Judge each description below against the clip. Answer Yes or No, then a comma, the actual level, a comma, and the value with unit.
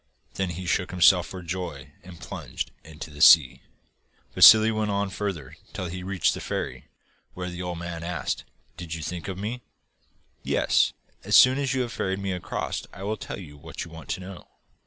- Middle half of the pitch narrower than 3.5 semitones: Yes, average, 2.7 semitones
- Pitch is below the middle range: Yes, very low, 90 Hz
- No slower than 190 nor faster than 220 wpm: Yes, average, 200 wpm